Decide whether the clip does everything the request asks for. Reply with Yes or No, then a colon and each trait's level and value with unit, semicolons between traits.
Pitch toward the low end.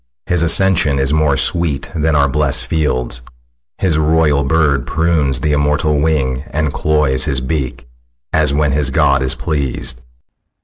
Yes: very low, 75 Hz